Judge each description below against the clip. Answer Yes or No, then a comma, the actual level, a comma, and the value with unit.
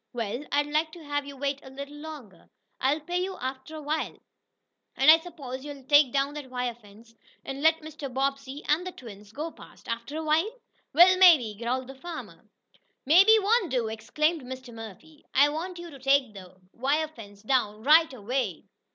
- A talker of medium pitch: No, very high, 280 Hz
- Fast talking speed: No, average, 190 wpm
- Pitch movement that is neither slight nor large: Yes, average, 4.0 semitones